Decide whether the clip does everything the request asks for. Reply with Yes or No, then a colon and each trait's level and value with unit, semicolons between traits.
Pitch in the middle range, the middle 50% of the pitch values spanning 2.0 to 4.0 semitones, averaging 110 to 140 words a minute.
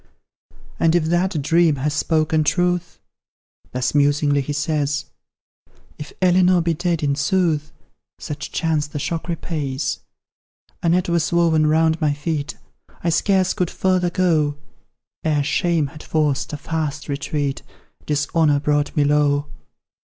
Yes: medium, 155 Hz; average, 2.7 semitones; slow, 135 wpm